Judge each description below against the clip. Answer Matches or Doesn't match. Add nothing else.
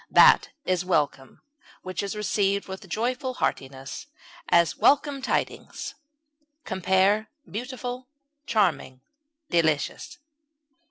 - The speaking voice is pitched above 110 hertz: Matches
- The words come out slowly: Matches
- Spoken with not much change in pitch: Doesn't match